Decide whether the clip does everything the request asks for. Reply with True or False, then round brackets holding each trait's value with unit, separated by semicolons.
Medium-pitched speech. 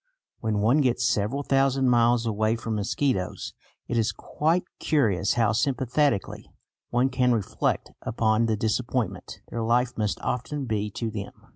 False (115 Hz)